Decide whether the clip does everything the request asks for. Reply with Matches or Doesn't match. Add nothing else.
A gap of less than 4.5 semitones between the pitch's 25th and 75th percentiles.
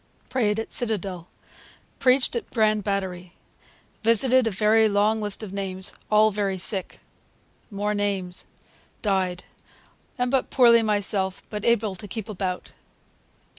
Matches